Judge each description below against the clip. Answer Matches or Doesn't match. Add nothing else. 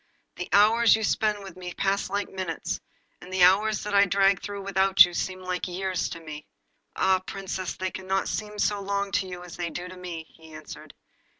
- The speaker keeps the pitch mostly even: Matches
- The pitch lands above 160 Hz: Matches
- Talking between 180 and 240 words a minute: Matches